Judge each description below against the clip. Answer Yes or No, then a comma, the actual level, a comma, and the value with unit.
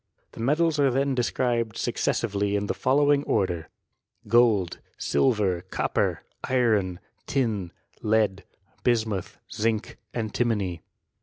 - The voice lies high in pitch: No, low, 110 Hz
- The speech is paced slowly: Yes, slow, 105 wpm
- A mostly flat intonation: No, average, 4.0 semitones